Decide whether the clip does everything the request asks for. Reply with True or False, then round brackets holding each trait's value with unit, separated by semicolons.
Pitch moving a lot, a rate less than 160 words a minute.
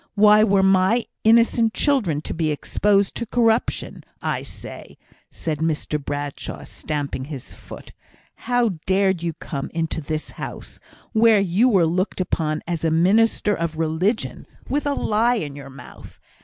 True (5.9 semitones; 150 wpm)